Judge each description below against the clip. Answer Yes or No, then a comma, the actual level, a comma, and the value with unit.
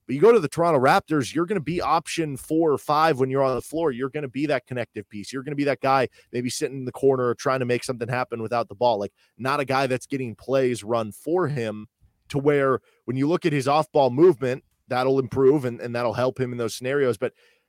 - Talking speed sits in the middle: No, fast, 265 wpm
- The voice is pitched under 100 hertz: No, low, 135 Hz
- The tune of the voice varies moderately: Yes, average, 3.6 semitones